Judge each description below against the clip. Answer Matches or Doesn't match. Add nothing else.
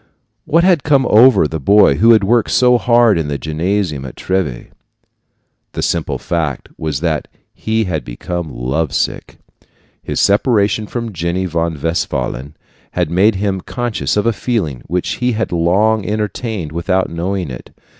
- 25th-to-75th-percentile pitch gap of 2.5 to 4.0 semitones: Doesn't match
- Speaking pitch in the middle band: Doesn't match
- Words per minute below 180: Matches